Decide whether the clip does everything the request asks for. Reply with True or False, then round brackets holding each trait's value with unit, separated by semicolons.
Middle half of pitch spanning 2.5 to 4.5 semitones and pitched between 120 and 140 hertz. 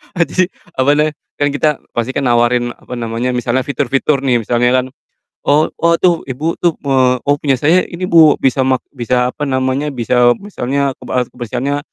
True (3.1 semitones; 135 Hz)